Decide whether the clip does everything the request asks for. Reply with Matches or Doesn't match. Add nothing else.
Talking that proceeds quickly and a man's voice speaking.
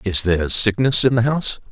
Matches